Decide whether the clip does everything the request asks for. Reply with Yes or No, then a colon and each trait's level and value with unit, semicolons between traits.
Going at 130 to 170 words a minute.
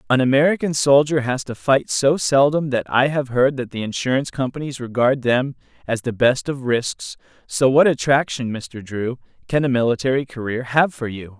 No: average, 185 wpm